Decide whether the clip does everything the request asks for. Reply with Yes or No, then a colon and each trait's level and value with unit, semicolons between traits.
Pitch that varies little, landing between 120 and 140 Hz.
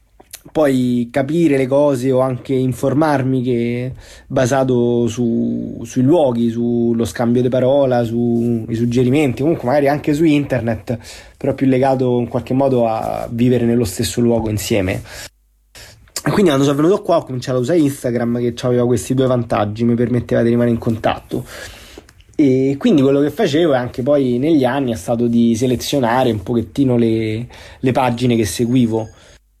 Yes: narrow, 2.3 semitones; low, 125 Hz